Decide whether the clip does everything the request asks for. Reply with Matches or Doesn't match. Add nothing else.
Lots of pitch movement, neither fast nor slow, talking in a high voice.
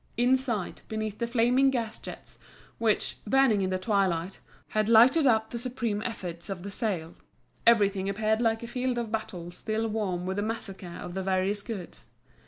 Doesn't match